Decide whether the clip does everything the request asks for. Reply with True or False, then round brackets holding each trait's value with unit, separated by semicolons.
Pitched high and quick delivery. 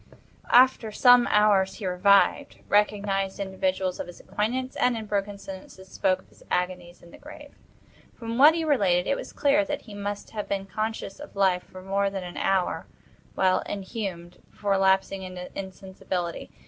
False (195 Hz; 170 wpm)